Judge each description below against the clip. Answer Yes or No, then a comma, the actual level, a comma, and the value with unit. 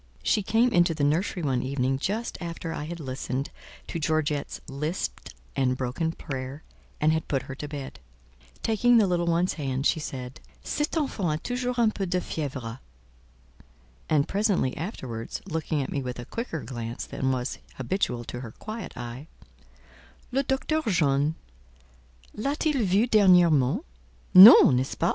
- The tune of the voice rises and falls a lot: Yes, wide, 6.8 semitones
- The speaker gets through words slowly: No, average, 160 wpm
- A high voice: No, medium, 155 Hz